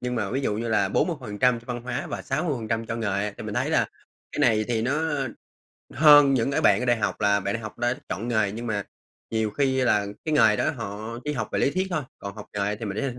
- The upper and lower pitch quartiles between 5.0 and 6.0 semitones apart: No, average, 3.5 semitones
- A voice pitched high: No, low, 115 Hz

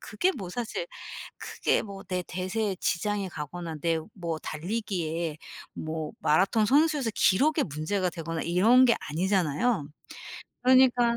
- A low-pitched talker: No, medium, 185 Hz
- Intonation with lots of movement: Yes, wide, 5.9 semitones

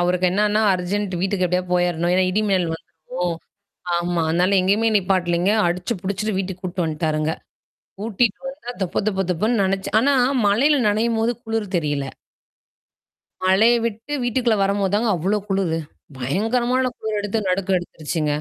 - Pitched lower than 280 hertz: Yes, high, 190 Hz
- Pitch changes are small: No, average, 3.4 semitones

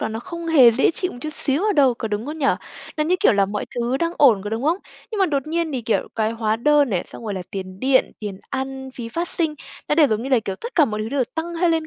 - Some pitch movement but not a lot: No, wide, 6.2 semitones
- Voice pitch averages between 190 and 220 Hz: No, very high, 265 Hz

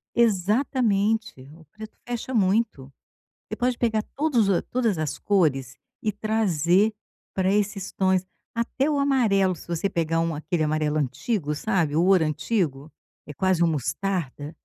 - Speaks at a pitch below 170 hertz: No, high, 190 Hz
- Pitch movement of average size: No, wide, 5.8 semitones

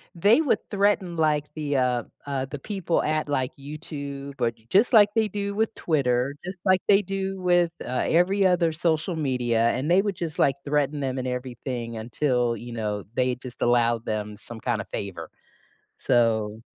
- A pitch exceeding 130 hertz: Yes, medium, 140 Hz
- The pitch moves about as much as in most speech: No, wide, 6.5 semitones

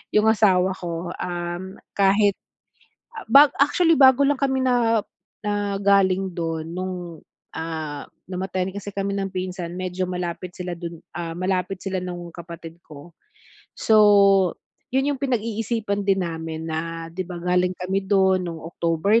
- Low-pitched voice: No, medium, 185 Hz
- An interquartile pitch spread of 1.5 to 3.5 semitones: Yes, average, 2.8 semitones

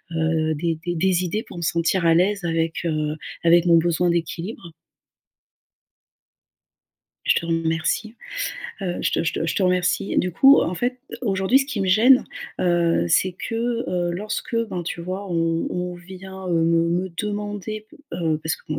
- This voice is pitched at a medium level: Yes, medium, 175 Hz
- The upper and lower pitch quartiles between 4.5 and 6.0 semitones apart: No, average, 2.7 semitones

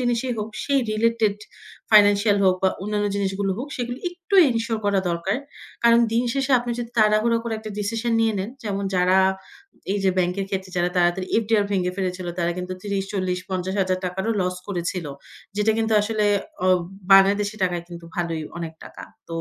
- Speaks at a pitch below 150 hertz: No, high, 200 Hz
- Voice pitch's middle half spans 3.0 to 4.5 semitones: Yes, average, 3.4 semitones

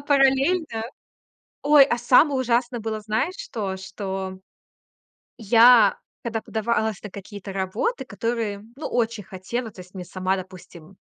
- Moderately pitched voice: No, high, 220 Hz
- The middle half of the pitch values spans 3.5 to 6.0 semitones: Yes, average, 4.4 semitones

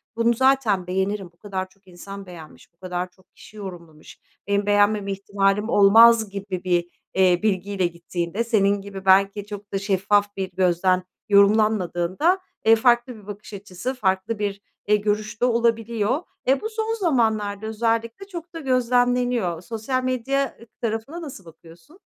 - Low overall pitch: No, high, 205 Hz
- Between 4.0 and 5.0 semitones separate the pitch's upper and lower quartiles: No, average, 3.6 semitones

